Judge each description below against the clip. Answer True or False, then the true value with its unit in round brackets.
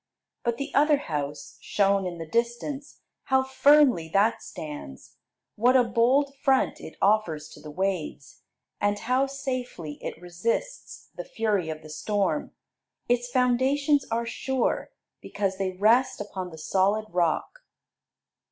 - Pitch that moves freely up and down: True (6.6 semitones)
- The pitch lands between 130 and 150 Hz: False (220 Hz)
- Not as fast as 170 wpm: True (135 wpm)